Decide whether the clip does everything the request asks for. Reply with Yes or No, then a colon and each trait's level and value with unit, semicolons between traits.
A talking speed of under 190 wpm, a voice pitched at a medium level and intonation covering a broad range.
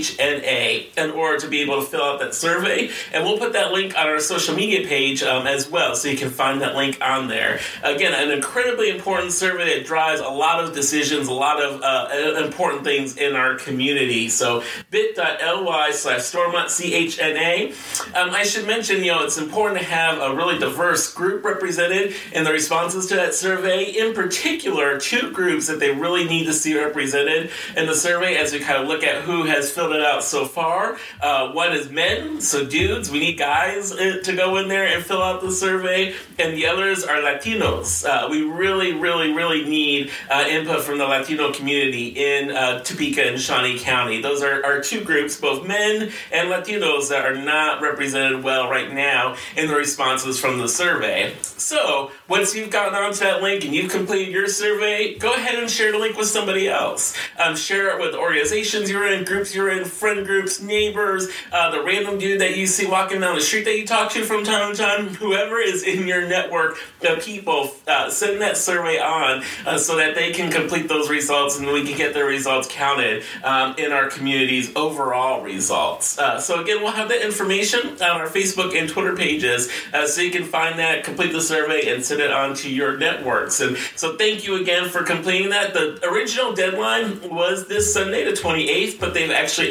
No: average, 200 wpm; medium, 175 Hz; wide, 5.7 semitones